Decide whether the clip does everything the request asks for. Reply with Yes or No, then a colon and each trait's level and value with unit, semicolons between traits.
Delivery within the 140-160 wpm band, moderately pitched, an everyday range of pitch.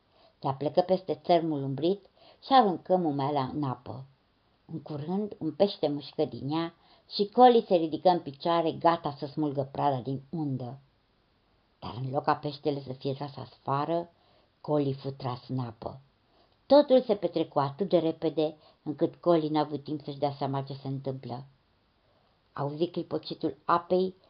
Yes: average, 155 wpm; medium, 150 Hz; average, 3.8 semitones